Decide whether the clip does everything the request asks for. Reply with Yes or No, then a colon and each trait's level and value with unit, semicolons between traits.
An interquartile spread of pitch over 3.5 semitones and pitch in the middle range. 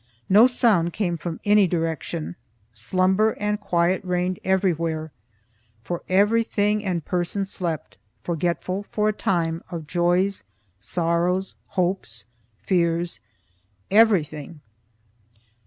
No: average, 2.9 semitones; medium, 180 Hz